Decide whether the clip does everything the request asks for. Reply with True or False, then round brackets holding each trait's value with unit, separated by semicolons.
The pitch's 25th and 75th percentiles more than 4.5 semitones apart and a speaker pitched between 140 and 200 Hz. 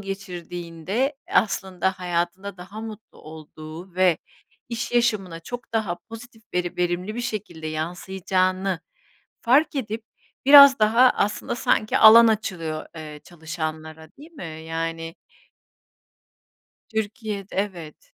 True (4.9 semitones; 190 Hz)